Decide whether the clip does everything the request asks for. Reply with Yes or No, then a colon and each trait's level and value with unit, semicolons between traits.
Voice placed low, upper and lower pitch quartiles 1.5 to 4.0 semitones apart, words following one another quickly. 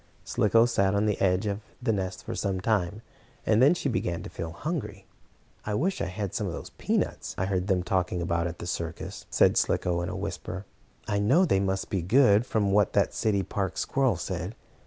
Yes: low, 100 Hz; average, 3.2 semitones; fast, 210 wpm